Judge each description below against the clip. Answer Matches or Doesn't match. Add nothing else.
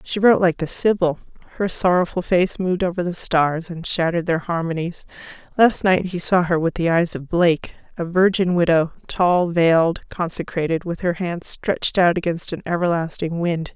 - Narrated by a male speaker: Doesn't match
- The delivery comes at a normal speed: Matches